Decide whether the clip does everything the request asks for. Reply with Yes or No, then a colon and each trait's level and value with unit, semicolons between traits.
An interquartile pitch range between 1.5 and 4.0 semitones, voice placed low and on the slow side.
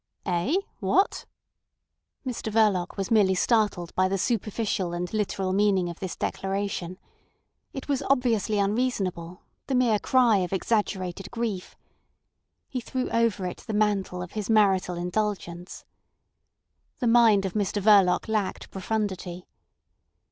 No: average, 3.2 semitones; high, 200 Hz; slow, 125 wpm